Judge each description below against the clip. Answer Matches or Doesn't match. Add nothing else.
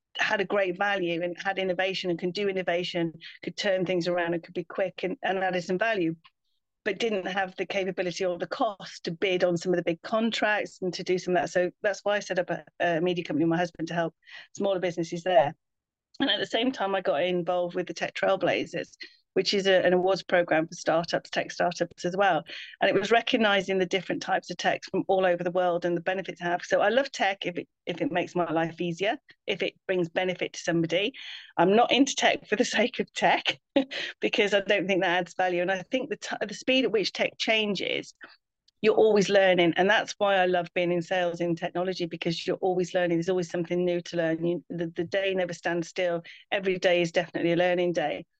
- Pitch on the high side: Doesn't match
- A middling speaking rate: Doesn't match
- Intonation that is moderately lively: Doesn't match